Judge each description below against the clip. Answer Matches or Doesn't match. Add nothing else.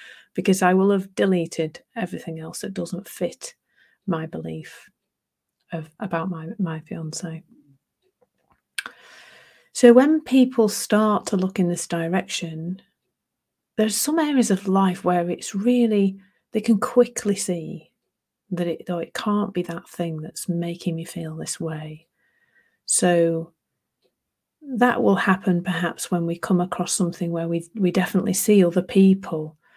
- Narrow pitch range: Doesn't match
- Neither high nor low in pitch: Matches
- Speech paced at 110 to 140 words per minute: Matches